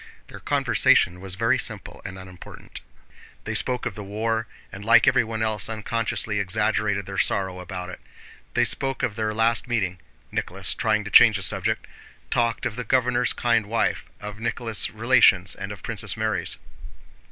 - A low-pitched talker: Yes, low, 110 Hz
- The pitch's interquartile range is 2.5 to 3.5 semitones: Yes, average, 3.0 semitones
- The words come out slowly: No, average, 160 wpm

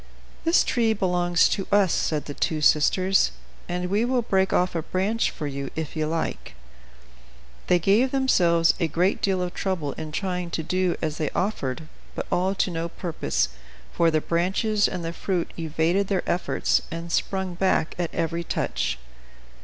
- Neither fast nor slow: Yes, average, 170 wpm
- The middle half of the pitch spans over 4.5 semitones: No, average, 2.9 semitones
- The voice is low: No, medium, 175 Hz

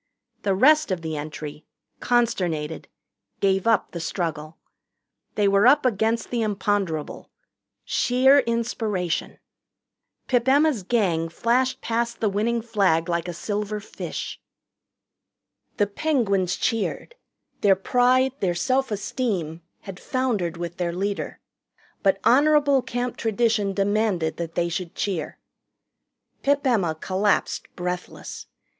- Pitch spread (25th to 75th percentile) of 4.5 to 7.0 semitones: Yes, average, 5.3 semitones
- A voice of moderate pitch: No, high, 205 Hz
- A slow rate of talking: Yes, slow, 115 wpm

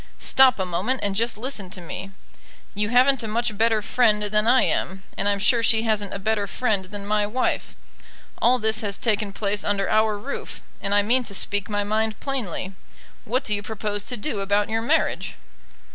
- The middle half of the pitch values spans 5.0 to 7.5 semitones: No, narrow, 2.4 semitones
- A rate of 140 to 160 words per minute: No, average, 200 wpm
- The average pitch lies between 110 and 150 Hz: No, high, 210 Hz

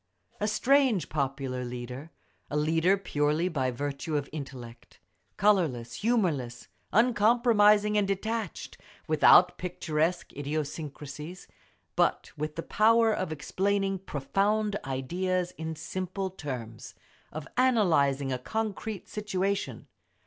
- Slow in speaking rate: Yes, slow, 100 wpm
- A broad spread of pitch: Yes, wide, 6.4 semitones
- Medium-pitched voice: Yes, medium, 170 Hz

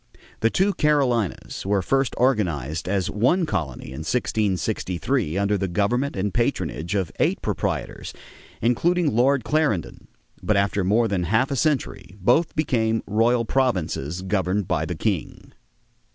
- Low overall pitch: Yes, low, 105 Hz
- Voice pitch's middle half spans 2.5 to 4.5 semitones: No, wide, 5.5 semitones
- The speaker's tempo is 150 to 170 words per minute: No, average, 140 wpm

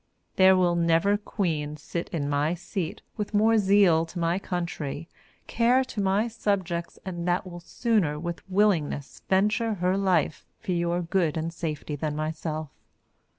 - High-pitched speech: No, medium, 175 Hz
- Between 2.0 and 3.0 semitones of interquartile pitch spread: No, average, 3.5 semitones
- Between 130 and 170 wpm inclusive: Yes, average, 150 wpm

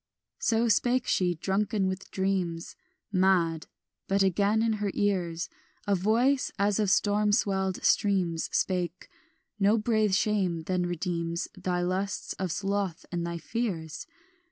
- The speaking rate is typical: No, slow, 130 wpm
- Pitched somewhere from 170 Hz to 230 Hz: Yes, high, 190 Hz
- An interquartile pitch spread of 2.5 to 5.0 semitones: Yes, average, 2.8 semitones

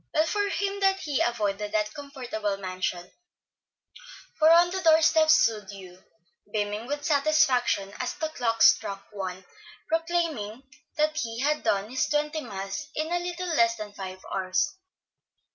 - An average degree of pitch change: No, wide, 7.5 semitones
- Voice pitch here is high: Yes, very high, 250 Hz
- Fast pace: No, average, 150 wpm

